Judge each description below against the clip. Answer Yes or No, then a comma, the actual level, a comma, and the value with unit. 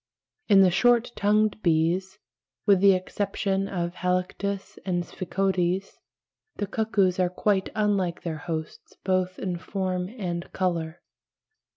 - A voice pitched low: No, medium, 185 Hz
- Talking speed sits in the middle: No, slow, 120 wpm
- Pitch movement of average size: No, narrow, 2.1 semitones